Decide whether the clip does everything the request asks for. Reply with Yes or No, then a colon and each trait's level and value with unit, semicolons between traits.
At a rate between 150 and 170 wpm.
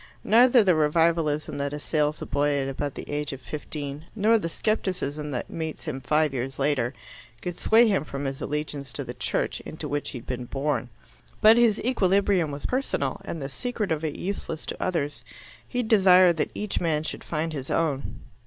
No: average, 190 wpm